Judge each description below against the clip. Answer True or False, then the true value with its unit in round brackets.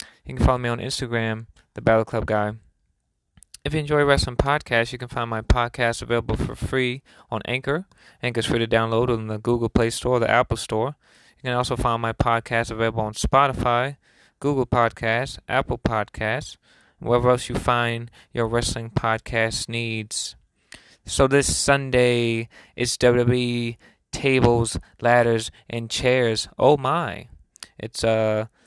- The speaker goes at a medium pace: True (155 wpm)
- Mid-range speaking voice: False (120 Hz)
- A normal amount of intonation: False (1.9 semitones)